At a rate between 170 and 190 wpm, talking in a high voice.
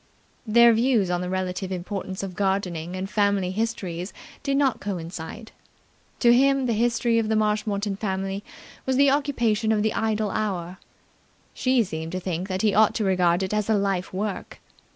Yes: average, 175 wpm; high, 205 Hz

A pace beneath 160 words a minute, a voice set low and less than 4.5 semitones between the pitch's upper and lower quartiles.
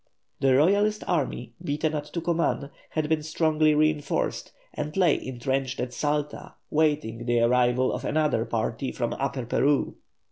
No: average, 140 wpm; medium, 145 Hz; average, 3.6 semitones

